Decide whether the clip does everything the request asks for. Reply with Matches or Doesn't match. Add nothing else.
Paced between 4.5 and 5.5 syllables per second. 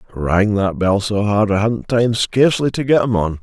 Matches